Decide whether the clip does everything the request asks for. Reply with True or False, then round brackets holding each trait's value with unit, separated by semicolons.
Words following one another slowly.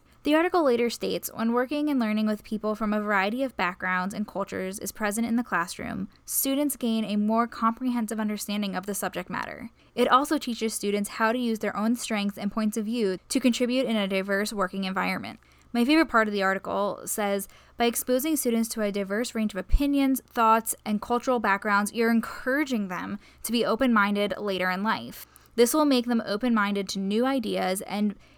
False (195 wpm)